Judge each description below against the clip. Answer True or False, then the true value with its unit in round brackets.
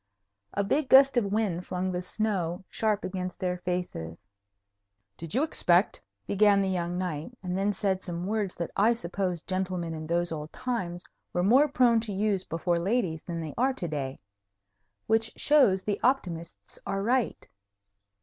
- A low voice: False (185 Hz)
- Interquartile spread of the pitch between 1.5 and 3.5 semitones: False (4.0 semitones)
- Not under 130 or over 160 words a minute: False (170 wpm)